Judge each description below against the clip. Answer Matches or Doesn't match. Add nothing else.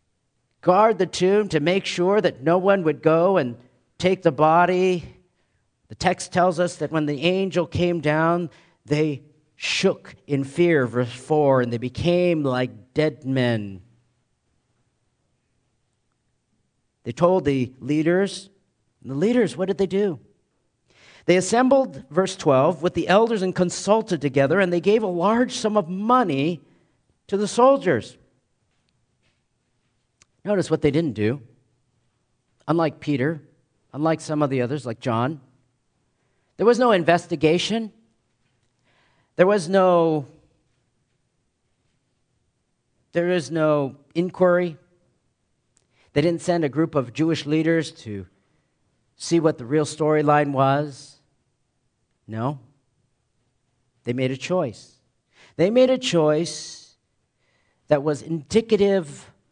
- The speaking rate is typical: Doesn't match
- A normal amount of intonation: Doesn't match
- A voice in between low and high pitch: Matches